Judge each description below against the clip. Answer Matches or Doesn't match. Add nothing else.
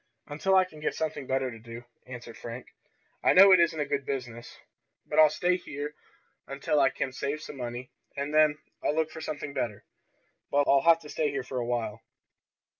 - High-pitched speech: Doesn't match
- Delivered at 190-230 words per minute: Matches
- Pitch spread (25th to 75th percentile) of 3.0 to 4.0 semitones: Matches